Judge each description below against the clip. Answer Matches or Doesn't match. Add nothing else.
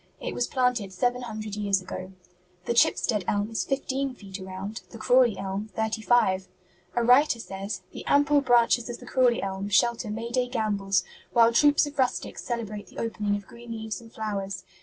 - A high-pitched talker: Matches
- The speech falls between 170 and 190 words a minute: Matches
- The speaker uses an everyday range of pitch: Matches